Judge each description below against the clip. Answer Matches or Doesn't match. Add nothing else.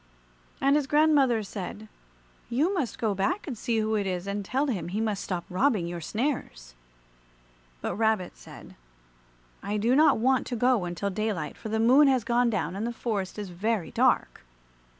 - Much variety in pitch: Doesn't match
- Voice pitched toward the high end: Matches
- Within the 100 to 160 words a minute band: Doesn't match